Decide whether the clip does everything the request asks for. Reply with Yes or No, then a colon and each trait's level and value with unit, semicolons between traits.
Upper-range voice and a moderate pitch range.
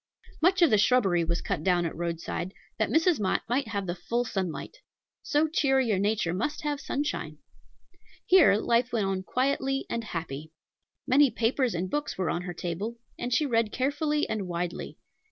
No: high, 220 Hz; wide, 7.1 semitones